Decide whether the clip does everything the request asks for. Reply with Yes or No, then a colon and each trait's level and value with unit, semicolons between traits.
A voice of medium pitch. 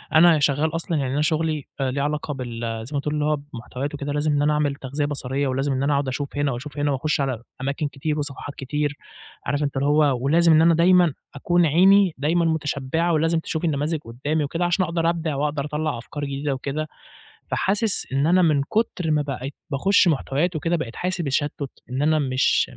Yes: medium, 145 Hz